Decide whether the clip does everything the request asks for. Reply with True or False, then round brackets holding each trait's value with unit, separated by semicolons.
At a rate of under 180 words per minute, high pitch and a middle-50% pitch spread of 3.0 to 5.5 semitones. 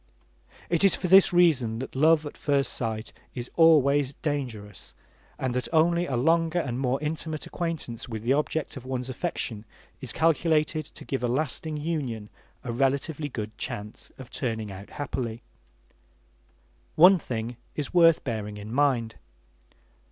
False (150 wpm; 135 Hz; 5.1 semitones)